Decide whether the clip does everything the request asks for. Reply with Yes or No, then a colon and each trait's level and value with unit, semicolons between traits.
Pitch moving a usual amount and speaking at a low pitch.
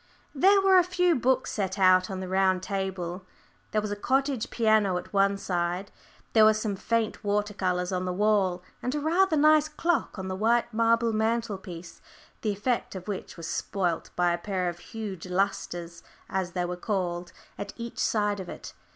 No: average, 4.0 semitones; high, 200 Hz